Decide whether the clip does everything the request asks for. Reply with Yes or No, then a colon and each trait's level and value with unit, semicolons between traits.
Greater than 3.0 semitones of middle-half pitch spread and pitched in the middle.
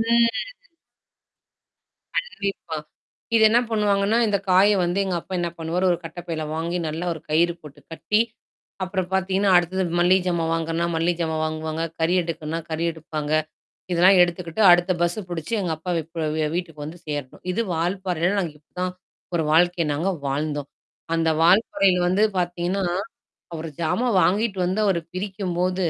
No: narrow, 2.5 semitones; medium, 175 Hz